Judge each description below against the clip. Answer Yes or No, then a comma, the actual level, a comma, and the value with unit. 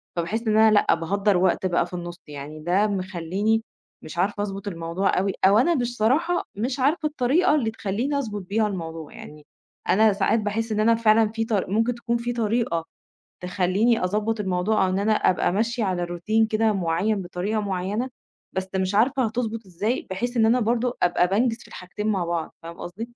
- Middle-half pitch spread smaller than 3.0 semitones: No, average, 3.7 semitones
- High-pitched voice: Yes, high, 210 Hz